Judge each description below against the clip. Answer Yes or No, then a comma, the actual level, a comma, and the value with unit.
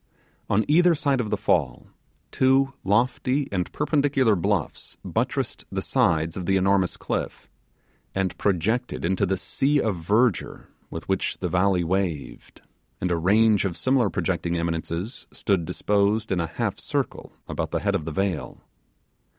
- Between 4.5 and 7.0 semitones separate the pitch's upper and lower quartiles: Yes, wide, 5.6 semitones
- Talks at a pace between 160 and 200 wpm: No, average, 150 wpm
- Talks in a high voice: No, low, 100 Hz